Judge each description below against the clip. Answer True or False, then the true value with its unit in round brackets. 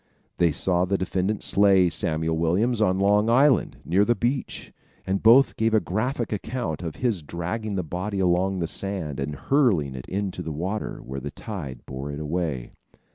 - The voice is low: True (95 Hz)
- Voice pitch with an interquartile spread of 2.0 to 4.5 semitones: False (4.9 semitones)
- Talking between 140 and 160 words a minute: False (180 wpm)